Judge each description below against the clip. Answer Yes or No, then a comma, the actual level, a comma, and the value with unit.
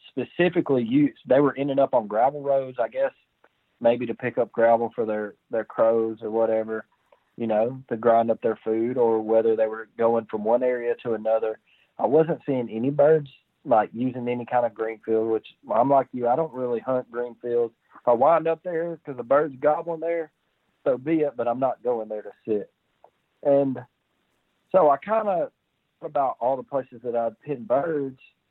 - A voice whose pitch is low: Yes, low, 125 Hz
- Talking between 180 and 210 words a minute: Yes, average, 190 wpm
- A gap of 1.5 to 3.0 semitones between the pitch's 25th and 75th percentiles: No, average, 4.1 semitones